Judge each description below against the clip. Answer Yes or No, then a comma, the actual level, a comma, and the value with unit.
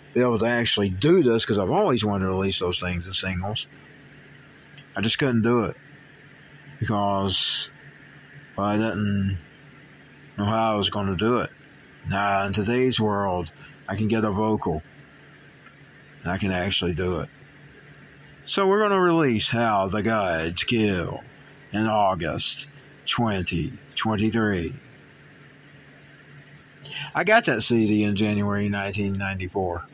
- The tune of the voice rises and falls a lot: Yes, wide, 5.9 semitones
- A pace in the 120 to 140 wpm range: Yes, slow, 135 wpm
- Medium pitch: No, low, 110 Hz